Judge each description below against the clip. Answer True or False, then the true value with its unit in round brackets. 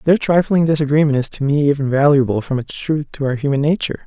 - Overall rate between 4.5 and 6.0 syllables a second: False (6.5 syllables/s)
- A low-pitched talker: False (145 Hz)